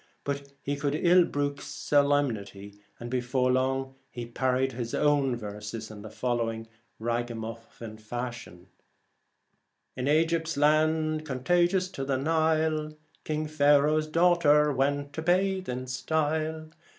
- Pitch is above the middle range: No, medium, 140 Hz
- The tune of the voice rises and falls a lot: No, average, 4.2 semitones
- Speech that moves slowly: Yes, slow, 120 wpm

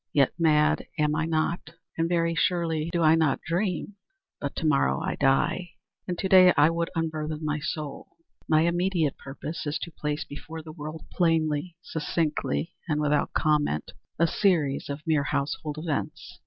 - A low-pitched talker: No, medium, 155 Hz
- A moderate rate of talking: Yes, average, 160 wpm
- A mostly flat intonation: Yes, narrow, 2.0 semitones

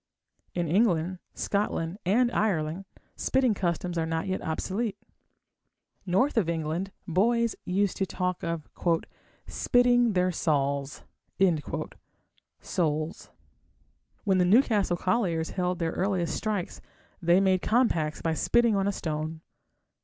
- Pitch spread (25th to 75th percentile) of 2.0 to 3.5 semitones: No, average, 3.9 semitones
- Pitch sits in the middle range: Yes, medium, 180 Hz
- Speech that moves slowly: Yes, slow, 115 wpm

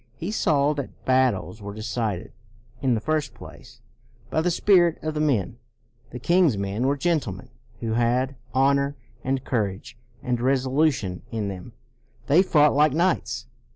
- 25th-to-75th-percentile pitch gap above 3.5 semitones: Yes, average, 4.8 semitones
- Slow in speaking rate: No, average, 155 wpm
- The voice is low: Yes, low, 130 Hz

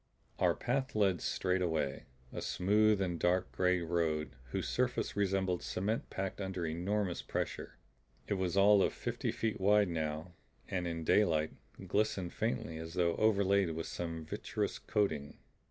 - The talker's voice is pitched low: Yes, very low, 90 Hz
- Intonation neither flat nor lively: Yes, average, 3.5 semitones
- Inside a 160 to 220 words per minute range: No, average, 150 wpm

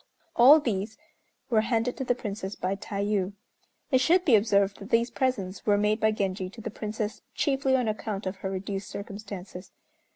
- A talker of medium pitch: No, high, 210 Hz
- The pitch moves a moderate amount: Yes, average, 3.0 semitones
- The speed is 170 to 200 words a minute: Yes, average, 175 wpm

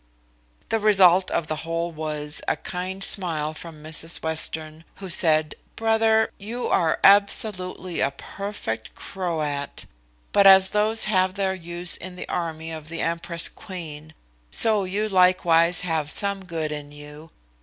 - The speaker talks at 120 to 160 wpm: Yes, average, 145 wpm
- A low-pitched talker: No, medium, 170 Hz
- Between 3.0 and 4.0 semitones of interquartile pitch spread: Yes, average, 3.5 semitones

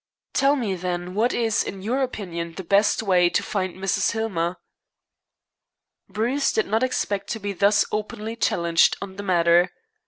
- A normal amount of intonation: Yes, average, 3.8 semitones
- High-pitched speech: Yes, high, 200 Hz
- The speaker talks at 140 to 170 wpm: Yes, average, 160 wpm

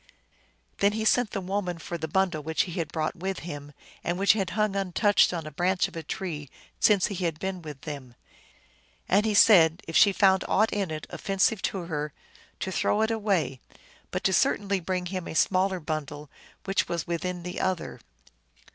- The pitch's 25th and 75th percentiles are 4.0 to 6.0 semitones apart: No, average, 3.5 semitones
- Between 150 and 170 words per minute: No, average, 190 wpm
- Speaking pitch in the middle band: Yes, medium, 180 Hz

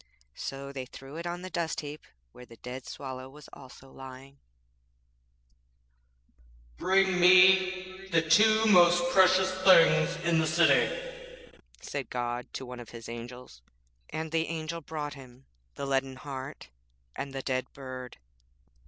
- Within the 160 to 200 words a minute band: No, average, 140 wpm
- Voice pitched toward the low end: No, medium, 150 Hz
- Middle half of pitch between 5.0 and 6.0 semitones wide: Yes, wide, 5.6 semitones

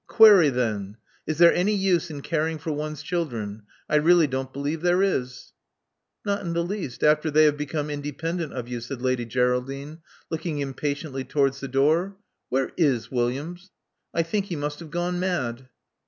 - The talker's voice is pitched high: No, medium, 150 Hz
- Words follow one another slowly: No, average, 170 wpm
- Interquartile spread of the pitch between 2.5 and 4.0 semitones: No, average, 4.4 semitones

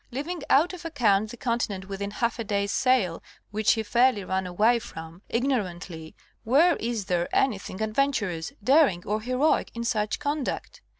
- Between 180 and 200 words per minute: No, average, 165 wpm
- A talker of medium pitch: No, high, 220 Hz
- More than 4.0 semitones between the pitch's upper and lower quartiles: Yes, average, 4.9 semitones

